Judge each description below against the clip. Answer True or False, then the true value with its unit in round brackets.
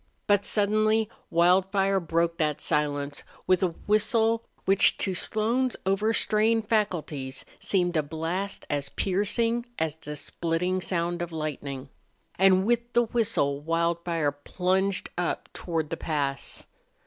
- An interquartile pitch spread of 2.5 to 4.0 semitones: False (4.7 semitones)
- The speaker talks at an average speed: False (125 wpm)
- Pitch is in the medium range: True (180 Hz)